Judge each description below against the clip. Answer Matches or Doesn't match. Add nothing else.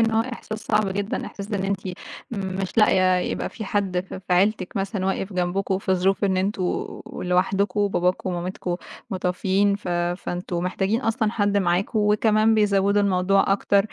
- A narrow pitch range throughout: Matches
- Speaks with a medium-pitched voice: Doesn't match